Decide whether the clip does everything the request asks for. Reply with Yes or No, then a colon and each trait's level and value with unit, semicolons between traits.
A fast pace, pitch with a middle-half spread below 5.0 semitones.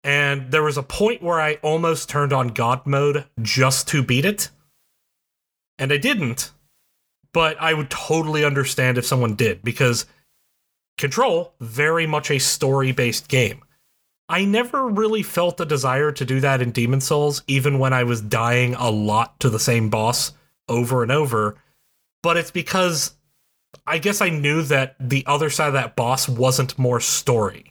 No: average, 165 wpm; average, 3.3 semitones